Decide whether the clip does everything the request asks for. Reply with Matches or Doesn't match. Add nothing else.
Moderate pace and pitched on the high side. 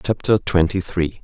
Doesn't match